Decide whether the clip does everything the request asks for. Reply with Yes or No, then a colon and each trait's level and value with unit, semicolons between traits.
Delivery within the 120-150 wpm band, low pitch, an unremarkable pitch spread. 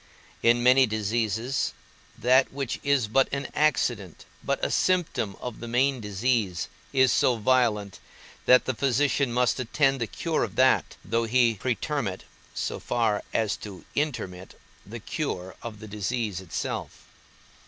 Yes: average, 145 wpm; low, 120 Hz; average, 3.8 semitones